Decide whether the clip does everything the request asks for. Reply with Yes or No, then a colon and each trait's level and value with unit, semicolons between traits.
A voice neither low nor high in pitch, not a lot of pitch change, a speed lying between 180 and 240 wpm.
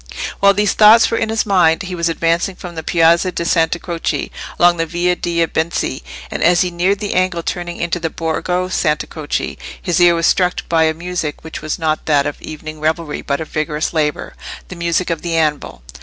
Yes: medium, 170 Hz; narrow, 2.0 semitones; fast, 205 wpm